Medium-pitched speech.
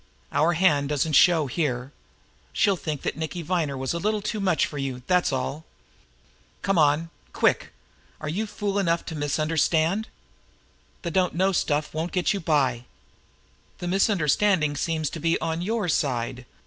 Yes: medium, 160 Hz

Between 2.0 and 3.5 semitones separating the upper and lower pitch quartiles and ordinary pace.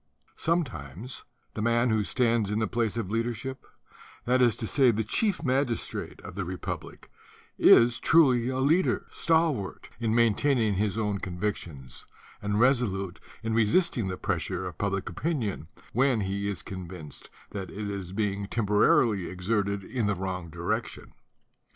No: average, 4.0 semitones; average, 150 wpm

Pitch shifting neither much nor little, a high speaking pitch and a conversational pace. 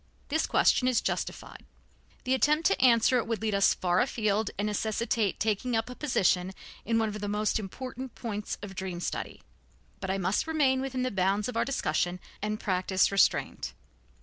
Yes: average, 4.3 semitones; high, 215 Hz; average, 180 wpm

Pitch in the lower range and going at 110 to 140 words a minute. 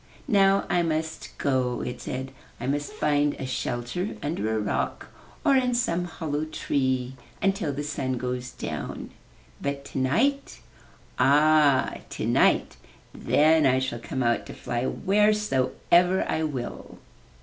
No: medium, 145 Hz; slow, 135 wpm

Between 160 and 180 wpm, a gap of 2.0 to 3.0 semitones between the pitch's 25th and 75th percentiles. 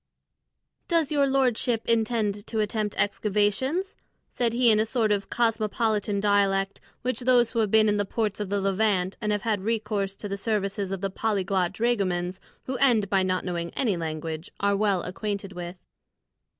Yes: average, 175 wpm; narrow, 2.6 semitones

